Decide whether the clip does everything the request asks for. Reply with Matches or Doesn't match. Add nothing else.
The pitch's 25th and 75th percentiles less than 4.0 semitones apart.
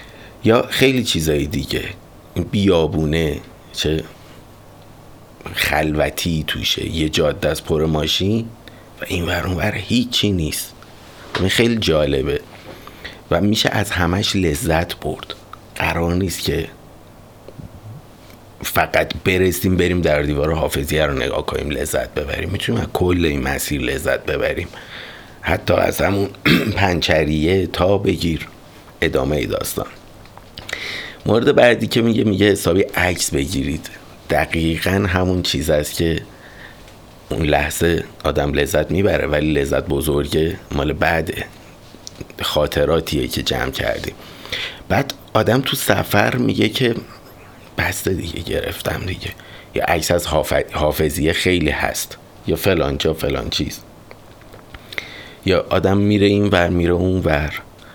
Doesn't match